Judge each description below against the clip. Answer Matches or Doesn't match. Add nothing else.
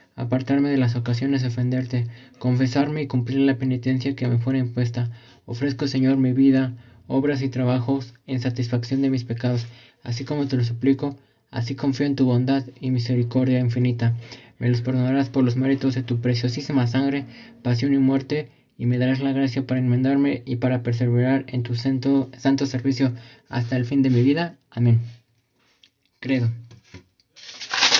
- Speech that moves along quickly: Doesn't match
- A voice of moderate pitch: Doesn't match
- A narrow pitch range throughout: Matches